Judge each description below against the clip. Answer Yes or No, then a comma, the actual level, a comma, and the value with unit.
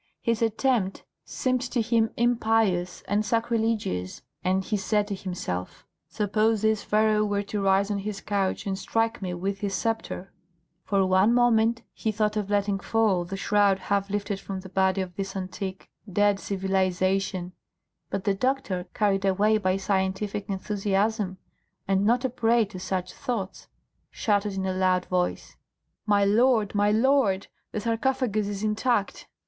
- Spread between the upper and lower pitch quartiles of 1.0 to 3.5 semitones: Yes, narrow, 2.5 semitones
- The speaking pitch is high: Yes, high, 205 Hz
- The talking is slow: No, average, 155 wpm